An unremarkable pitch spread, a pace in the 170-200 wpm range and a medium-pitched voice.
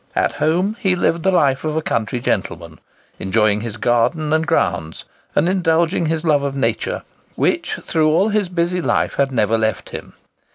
No: wide, 7.0 semitones; average, 175 wpm; medium, 155 Hz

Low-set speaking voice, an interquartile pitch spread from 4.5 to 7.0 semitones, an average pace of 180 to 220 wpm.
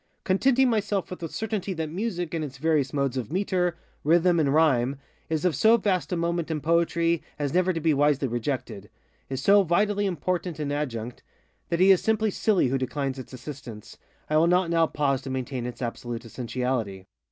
No: medium, 160 Hz; wide, 5.5 semitones; average, 185 wpm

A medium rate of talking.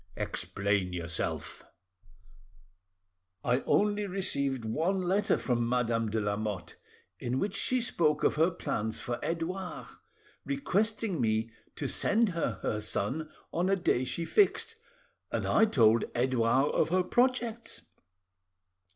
No: slow, 125 wpm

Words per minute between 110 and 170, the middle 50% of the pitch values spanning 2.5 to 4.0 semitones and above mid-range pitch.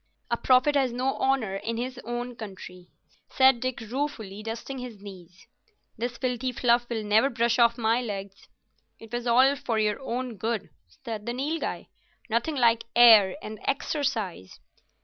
Yes: average, 155 wpm; average, 2.9 semitones; high, 235 Hz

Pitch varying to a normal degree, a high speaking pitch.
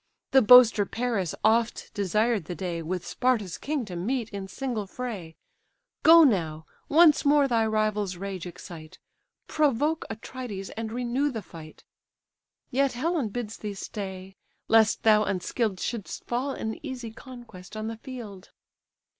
Yes: average, 4.6 semitones; high, 220 Hz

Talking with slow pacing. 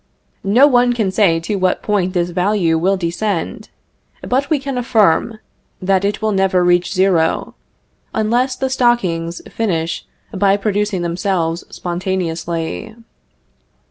Yes: slow, 125 wpm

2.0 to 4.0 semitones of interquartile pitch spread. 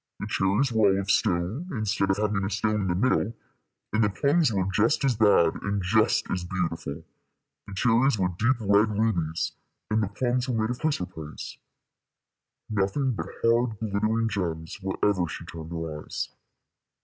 Yes: average, 3.4 semitones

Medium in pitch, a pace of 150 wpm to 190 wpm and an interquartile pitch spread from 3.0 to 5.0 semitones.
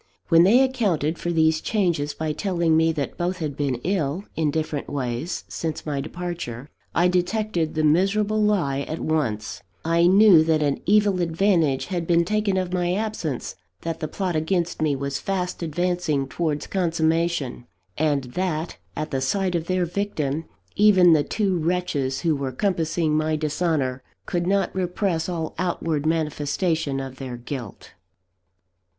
Yes: medium, 165 Hz; average, 155 wpm; average, 3.4 semitones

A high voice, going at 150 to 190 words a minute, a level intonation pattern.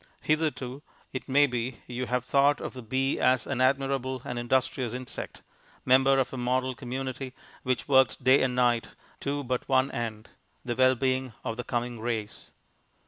No: low, 130 Hz; average, 170 wpm; narrow, 1.5 semitones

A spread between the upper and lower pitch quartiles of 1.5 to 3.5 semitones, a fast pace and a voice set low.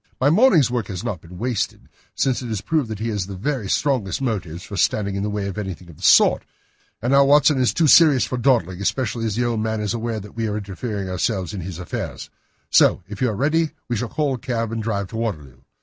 No: average, 4.4 semitones; fast, 250 wpm; low, 110 Hz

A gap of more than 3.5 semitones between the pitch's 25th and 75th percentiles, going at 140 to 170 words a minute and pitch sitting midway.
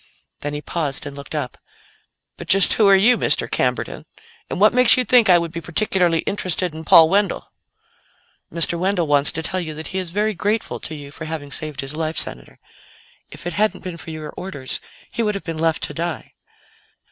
No: average, 4.0 semitones; fast, 205 wpm; medium, 170 Hz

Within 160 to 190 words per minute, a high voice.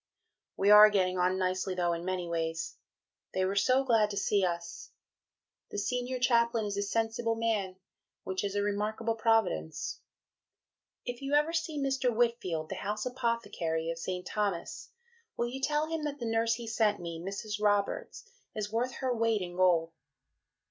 Yes: average, 170 wpm; high, 210 Hz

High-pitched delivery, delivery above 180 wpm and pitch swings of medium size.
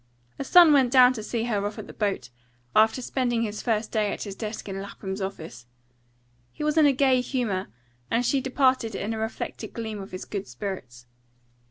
Yes: high, 220 Hz; average, 200 wpm; average, 4.2 semitones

